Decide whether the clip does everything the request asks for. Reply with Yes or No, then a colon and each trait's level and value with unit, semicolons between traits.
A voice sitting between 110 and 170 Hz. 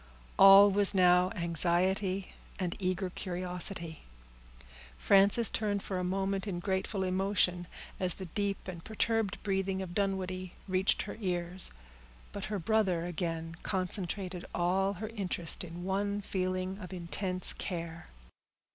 No: medium, 185 Hz